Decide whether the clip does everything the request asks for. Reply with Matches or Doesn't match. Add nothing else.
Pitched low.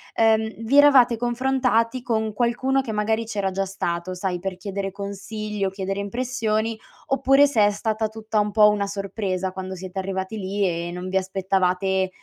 Doesn't match